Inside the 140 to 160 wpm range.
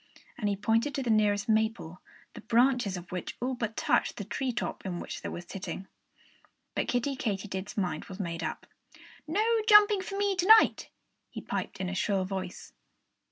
No: average, 185 wpm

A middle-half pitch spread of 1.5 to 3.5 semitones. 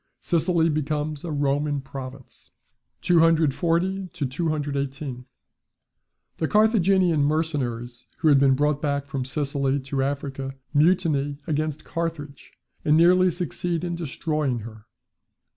Yes: average, 3.2 semitones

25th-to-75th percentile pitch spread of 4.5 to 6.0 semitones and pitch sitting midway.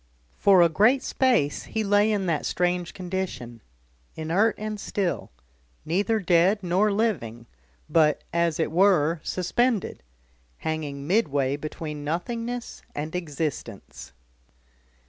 Yes: average, 5.1 semitones; medium, 175 Hz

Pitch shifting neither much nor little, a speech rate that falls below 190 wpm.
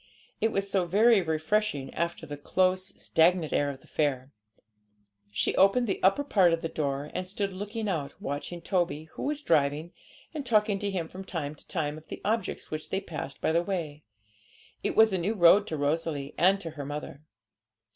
No: average, 4.7 semitones; average, 195 wpm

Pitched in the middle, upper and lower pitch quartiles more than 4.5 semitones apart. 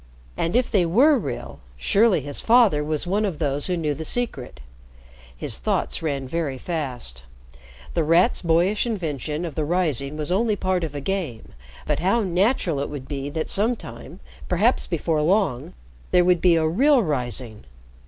Yes: medium, 165 Hz; average, 5.1 semitones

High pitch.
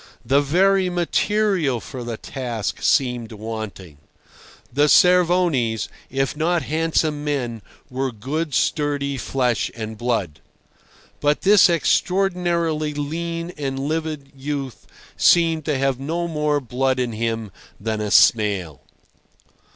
No: medium, 140 Hz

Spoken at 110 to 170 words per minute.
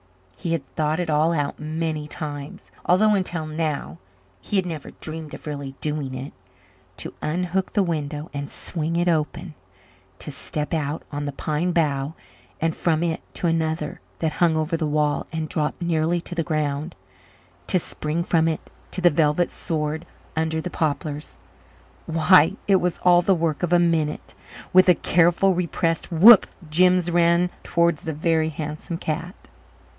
Yes: average, 165 wpm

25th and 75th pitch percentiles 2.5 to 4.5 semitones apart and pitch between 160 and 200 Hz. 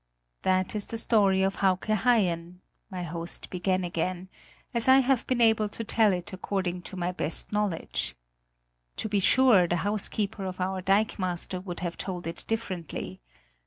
Yes: average, 3.2 semitones; high, 190 Hz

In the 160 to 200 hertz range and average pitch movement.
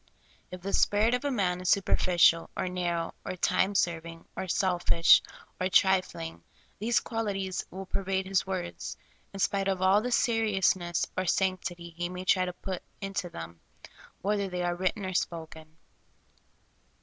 No: medium, 185 Hz; narrow, 2.0 semitones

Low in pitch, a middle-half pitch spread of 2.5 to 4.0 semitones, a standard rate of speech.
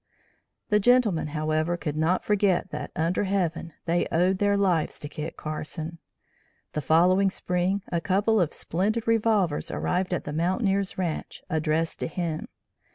No: medium, 180 Hz; average, 3.6 semitones; average, 150 wpm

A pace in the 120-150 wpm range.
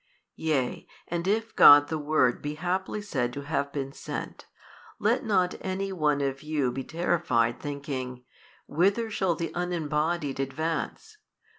Yes: average, 140 wpm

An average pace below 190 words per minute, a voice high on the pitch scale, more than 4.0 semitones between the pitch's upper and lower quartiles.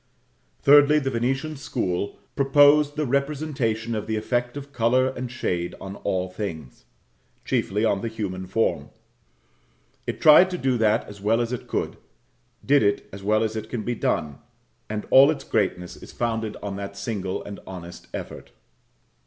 No: average, 165 wpm; low, 115 Hz; average, 5.1 semitones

